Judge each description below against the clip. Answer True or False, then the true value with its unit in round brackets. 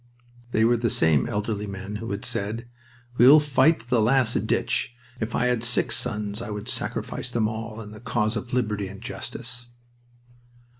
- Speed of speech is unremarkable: True (180 wpm)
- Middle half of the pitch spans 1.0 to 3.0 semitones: True (2.5 semitones)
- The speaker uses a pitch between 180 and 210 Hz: False (115 Hz)